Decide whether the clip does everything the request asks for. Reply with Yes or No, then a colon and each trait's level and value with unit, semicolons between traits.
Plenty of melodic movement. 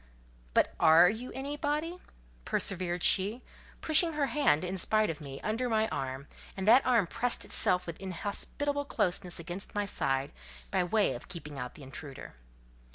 Yes: wide, 6.9 semitones